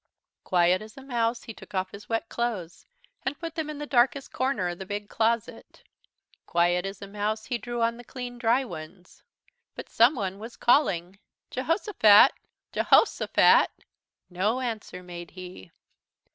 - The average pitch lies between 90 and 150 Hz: No, high, 220 Hz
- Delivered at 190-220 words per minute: No, average, 165 wpm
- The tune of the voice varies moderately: Yes, average, 4.9 semitones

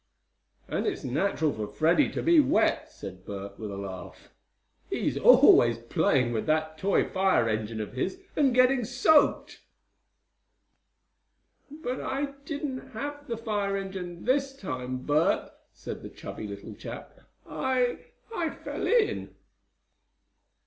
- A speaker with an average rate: No, slow, 130 wpm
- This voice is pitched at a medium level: No, high, 195 Hz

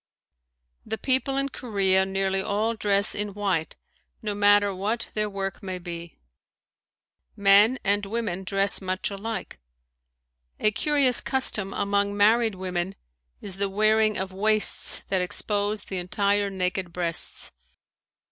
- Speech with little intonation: Yes, narrow, 2.0 semitones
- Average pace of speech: No, slow, 130 wpm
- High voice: Yes, high, 200 Hz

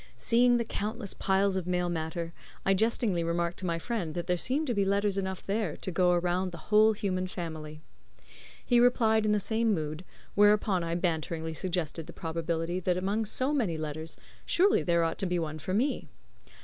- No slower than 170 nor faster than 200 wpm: Yes, average, 190 wpm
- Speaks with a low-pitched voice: No, medium, 185 Hz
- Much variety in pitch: No, average, 4.0 semitones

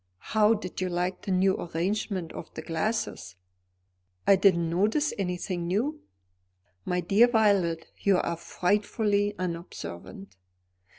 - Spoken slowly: Yes, slow, 120 wpm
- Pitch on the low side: No, medium, 185 Hz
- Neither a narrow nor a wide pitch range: Yes, average, 3.4 semitones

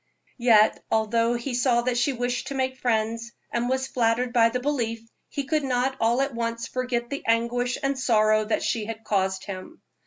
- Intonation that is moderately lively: No, narrow, 2.0 semitones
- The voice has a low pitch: No, high, 240 Hz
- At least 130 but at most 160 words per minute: No, average, 185 wpm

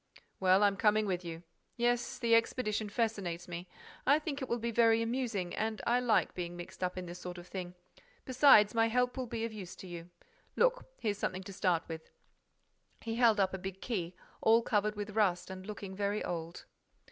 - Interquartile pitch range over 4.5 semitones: No, average, 4.1 semitones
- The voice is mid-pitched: No, high, 210 Hz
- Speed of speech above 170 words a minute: Yes, average, 195 wpm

